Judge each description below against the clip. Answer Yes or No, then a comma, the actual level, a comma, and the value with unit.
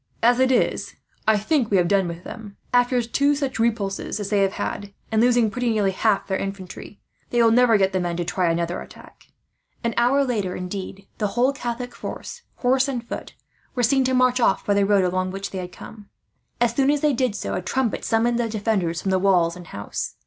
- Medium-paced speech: No, fast, 220 wpm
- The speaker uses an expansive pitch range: No, average, 4.3 semitones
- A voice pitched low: No, high, 215 Hz